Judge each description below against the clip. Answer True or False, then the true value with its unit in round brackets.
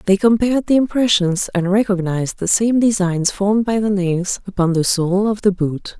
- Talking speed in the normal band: True (190 wpm)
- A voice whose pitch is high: True (200 Hz)